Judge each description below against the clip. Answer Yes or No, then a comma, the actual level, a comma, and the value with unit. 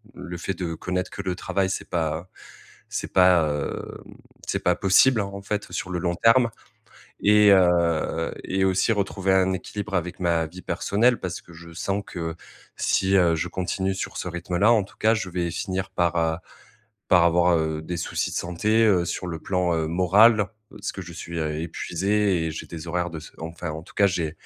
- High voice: No, very low, 90 Hz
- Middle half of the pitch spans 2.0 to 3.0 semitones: Yes, narrow, 2.6 semitones